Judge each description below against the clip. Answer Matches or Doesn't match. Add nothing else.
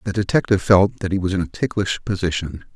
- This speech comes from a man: Matches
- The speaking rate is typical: Doesn't match